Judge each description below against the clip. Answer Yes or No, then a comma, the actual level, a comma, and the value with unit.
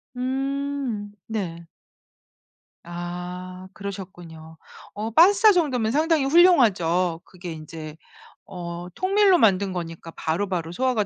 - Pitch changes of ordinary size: No, wide, 7.7 semitones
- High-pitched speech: Yes, high, 195 Hz